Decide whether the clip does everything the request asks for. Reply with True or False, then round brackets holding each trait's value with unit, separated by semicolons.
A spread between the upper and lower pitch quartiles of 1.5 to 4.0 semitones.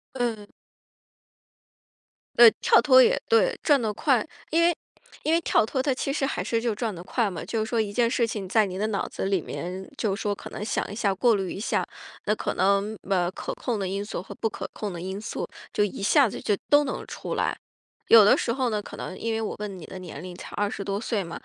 True (3.6 semitones)